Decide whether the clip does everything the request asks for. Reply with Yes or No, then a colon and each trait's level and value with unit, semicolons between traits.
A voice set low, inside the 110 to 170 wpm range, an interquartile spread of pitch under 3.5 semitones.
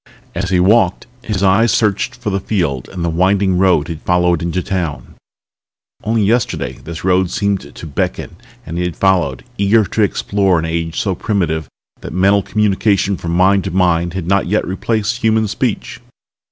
No: very low, 95 Hz; average, 180 wpm; average, 2.8 semitones